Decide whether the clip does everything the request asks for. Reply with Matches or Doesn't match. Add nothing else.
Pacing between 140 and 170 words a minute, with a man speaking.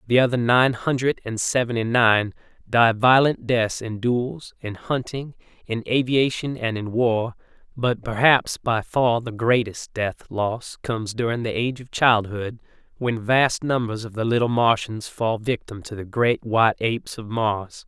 Matches